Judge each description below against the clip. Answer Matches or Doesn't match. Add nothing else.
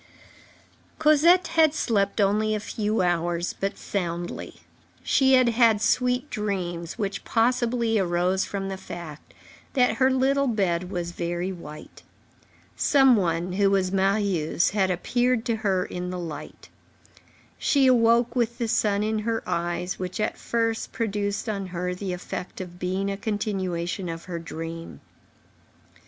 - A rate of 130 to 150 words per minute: Matches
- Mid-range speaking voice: Doesn't match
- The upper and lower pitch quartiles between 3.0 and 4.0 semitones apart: Doesn't match